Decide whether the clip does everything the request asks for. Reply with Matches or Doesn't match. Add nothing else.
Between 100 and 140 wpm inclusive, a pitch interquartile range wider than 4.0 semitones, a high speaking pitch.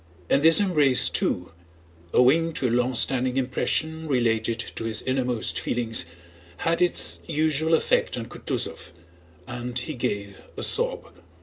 Doesn't match